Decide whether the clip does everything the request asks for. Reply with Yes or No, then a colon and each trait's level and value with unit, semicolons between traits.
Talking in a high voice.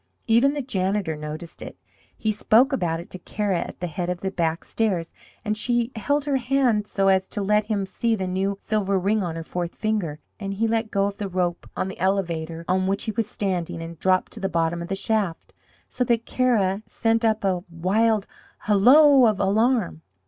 Yes: high, 195 Hz